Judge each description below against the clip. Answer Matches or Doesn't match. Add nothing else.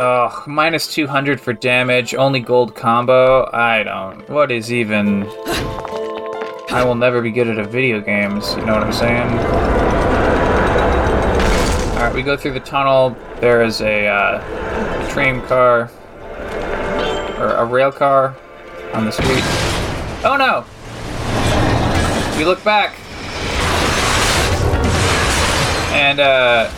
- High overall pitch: Doesn't match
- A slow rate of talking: Matches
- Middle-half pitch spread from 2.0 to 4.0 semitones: Doesn't match